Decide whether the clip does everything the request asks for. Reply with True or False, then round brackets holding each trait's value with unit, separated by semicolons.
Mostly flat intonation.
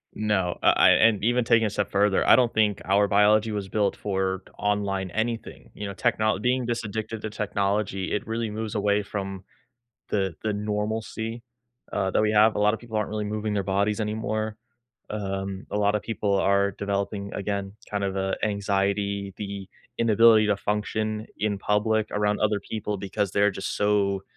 True (1.5 semitones)